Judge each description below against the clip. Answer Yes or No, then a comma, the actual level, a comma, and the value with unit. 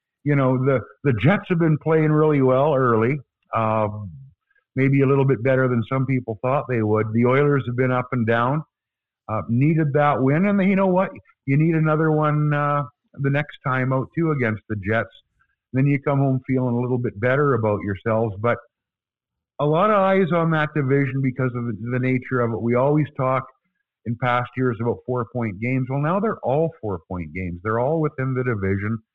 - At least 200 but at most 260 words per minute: Yes, fast, 205 wpm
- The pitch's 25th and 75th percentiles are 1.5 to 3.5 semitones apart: No, average, 3.9 semitones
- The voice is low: Yes, low, 130 Hz